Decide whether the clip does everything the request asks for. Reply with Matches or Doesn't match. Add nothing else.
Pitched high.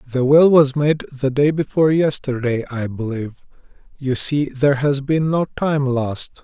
Doesn't match